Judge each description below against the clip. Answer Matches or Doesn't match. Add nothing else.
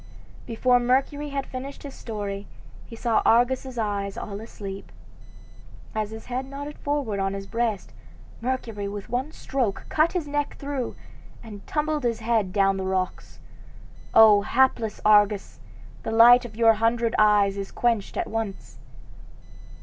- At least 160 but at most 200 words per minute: Doesn't match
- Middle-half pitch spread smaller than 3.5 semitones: Doesn't match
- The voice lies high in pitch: Matches